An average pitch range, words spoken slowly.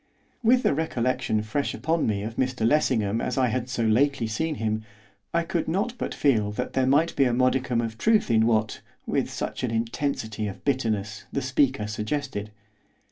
No: average, 4.4 semitones; average, 185 wpm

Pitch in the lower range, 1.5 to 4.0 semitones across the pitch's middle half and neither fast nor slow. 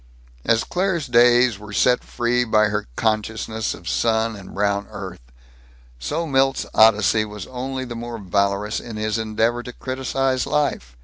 Yes: low, 115 Hz; average, 3.0 semitones; average, 150 wpm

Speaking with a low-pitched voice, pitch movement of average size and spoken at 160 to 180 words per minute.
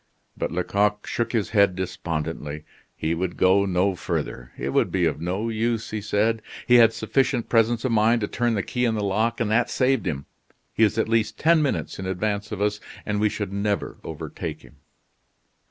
No: low, 105 Hz; average, 3.5 semitones; average, 200 wpm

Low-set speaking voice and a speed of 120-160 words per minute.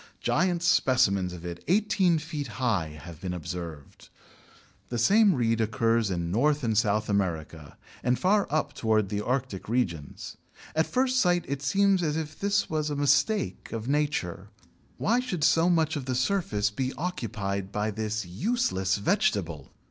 Yes: low, 125 Hz; average, 155 wpm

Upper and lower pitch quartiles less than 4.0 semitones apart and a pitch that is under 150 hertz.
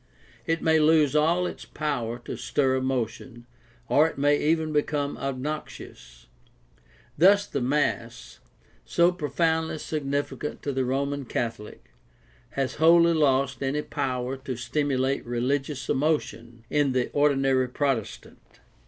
Yes: average, 2.9 semitones; medium, 140 Hz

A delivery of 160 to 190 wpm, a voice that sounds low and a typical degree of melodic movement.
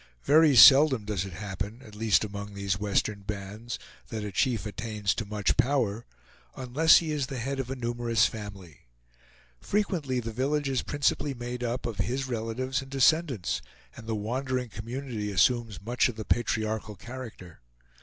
Yes: average, 165 wpm; low, 115 Hz; average, 3.9 semitones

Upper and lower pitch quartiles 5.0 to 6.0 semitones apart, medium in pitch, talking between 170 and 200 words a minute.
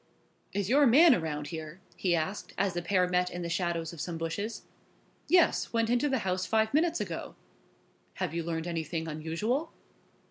Yes: wide, 5.6 semitones; medium, 180 Hz; average, 175 wpm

